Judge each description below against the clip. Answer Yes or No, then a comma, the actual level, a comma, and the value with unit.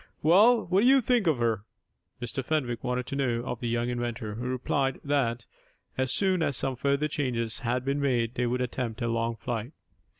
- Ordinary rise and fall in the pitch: Yes, average, 3.3 semitones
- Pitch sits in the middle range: No, low, 125 Hz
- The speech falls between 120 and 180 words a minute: No, average, 200 wpm